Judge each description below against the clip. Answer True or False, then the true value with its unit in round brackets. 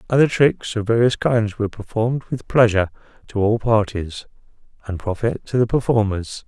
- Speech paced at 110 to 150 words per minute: False (160 wpm)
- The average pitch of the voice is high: False (110 Hz)